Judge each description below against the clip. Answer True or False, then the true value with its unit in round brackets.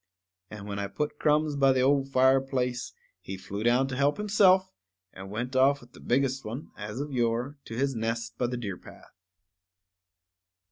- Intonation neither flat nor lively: True (3.5 semitones)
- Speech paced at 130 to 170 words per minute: False (185 wpm)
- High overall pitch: False (130 Hz)